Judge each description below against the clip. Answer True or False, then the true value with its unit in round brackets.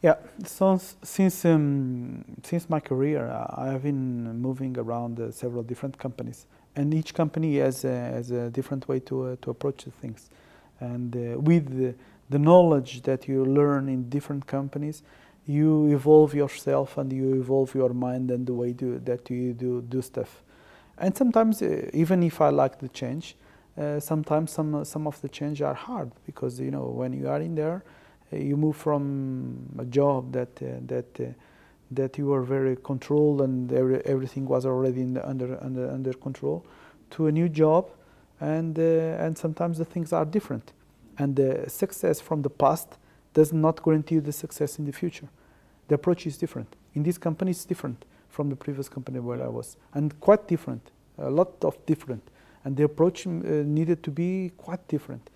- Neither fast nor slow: True (185 wpm)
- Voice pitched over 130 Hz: True (140 Hz)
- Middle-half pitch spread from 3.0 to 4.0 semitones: True (3.6 semitones)